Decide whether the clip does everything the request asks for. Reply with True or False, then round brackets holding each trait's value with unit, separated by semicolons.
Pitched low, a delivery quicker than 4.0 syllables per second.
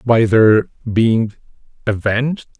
False (115 Hz; 3.2 syllables/s)